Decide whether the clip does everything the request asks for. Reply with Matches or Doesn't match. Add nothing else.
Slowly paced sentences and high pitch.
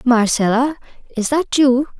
Matches